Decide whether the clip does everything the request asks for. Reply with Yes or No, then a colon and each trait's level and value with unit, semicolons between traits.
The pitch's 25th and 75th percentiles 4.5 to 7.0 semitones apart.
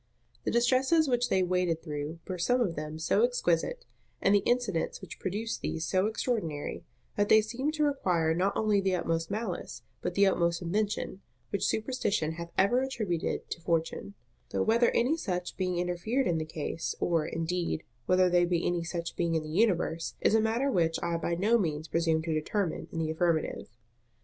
Yes: average, 4.9 semitones